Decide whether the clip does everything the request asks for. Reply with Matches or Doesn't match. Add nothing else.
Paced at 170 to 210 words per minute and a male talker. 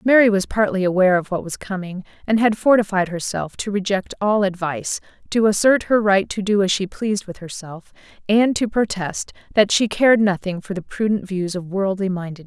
Doesn't match